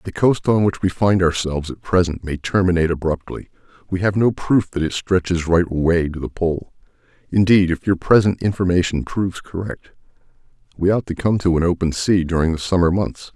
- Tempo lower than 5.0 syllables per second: No, 5.5 syllables/s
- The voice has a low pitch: Yes, very low, 90 Hz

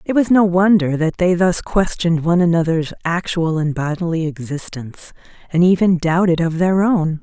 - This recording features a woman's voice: Yes, female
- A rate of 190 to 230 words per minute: No, average, 165 wpm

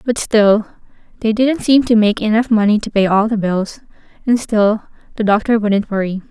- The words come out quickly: No, average, 180 wpm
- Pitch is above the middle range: Yes, high, 215 Hz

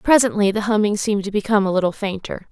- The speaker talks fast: Yes, fast, 215 wpm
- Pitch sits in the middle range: No, high, 205 Hz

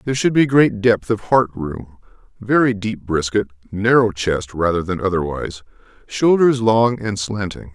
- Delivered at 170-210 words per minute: No, average, 155 wpm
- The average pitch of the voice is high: No, low, 105 Hz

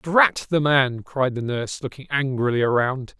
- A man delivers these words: Yes, male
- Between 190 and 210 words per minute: No, average, 170 wpm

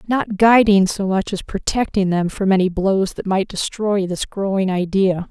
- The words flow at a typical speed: Yes, average, 180 wpm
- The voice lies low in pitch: No, high, 195 Hz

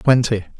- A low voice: Yes, low, 110 Hz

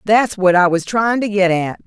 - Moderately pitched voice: No, high, 200 Hz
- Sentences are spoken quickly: Yes, fast, 255 wpm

